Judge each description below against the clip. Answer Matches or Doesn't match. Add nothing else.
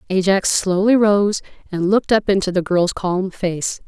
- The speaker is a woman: Matches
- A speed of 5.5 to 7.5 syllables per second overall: Doesn't match